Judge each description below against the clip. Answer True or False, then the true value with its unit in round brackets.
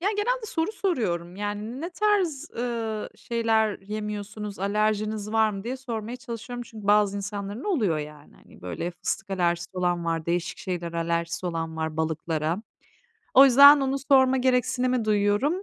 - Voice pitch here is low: False (210 Hz)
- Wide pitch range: True (6.1 semitones)